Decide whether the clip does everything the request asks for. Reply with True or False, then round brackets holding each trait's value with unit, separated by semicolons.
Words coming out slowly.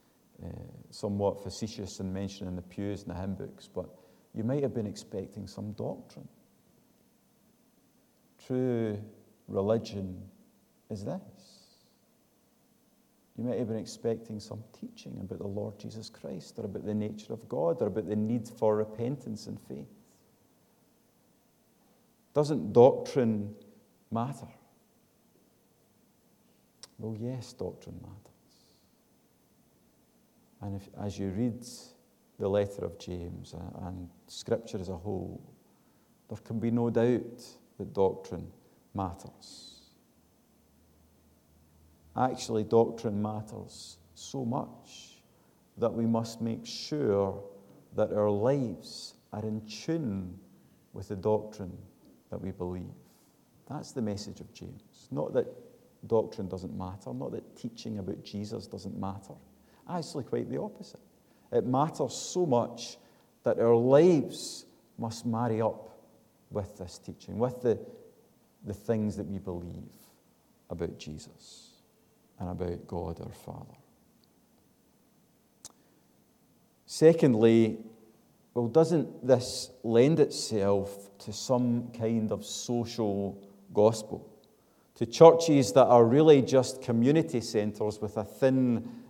True (115 wpm)